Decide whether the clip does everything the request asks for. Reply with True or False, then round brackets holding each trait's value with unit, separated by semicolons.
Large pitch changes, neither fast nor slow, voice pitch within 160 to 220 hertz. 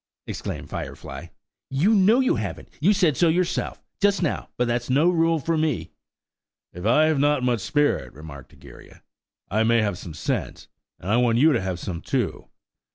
False (7.4 semitones; 175 wpm; 135 Hz)